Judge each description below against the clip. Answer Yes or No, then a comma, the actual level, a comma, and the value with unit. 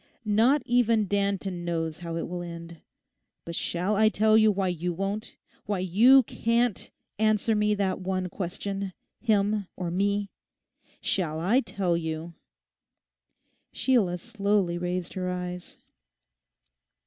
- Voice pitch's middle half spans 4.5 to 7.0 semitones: No, average, 3.3 semitones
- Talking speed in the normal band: No, slow, 125 wpm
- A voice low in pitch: No, high, 195 Hz